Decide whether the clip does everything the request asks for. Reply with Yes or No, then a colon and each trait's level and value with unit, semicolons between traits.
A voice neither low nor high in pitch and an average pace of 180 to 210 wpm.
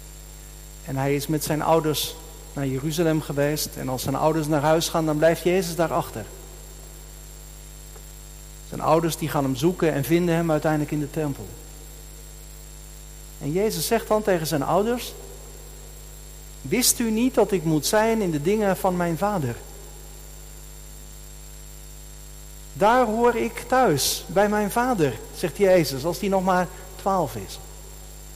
No: medium, 160 Hz; average, 145 wpm